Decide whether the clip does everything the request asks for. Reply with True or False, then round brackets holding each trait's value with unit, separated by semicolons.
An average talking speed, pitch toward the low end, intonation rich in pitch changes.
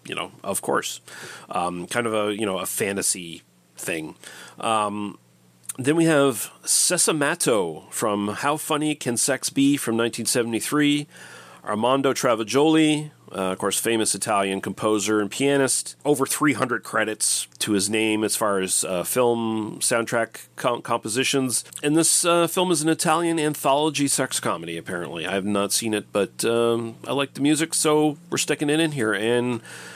True (160 wpm; 120 Hz; 5.8 semitones)